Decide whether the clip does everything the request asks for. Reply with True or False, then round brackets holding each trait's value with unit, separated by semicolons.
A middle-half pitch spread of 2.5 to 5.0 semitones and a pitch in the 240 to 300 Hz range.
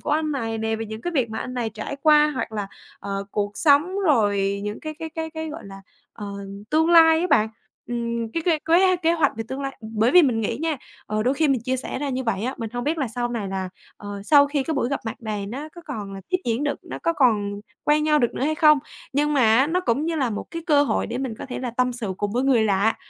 False (5.6 semitones; 255 Hz)